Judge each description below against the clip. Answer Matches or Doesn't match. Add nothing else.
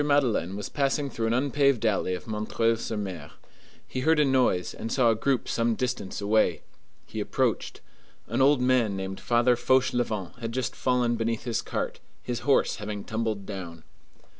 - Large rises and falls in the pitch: Doesn't match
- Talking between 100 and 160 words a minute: Doesn't match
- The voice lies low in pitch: Matches